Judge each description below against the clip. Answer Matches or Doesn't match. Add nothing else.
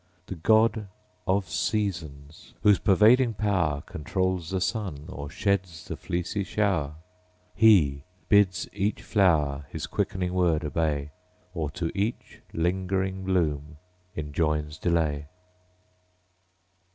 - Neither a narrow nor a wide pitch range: Matches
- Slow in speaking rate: Matches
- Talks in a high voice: Doesn't match